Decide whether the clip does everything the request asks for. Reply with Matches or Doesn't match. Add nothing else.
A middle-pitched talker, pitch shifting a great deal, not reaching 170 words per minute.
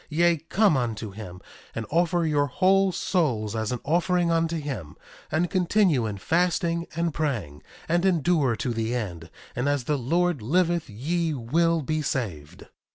Matches